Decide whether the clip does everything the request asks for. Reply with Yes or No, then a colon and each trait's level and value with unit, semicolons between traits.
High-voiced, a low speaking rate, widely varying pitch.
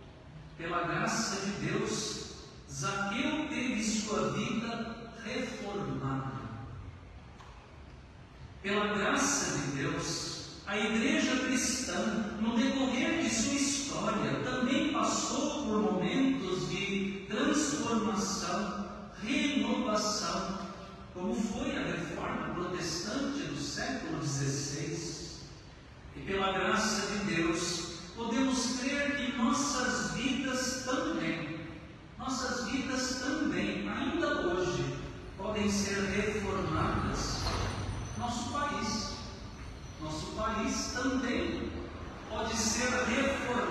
Yes: high, 220 Hz; slow, 85 wpm; wide, 6.0 semitones